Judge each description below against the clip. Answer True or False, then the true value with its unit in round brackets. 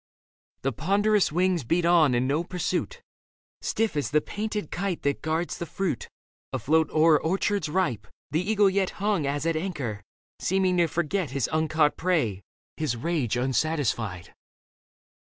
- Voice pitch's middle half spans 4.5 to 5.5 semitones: True (4.8 semitones)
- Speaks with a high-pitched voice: False (160 Hz)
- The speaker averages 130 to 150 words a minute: True (145 wpm)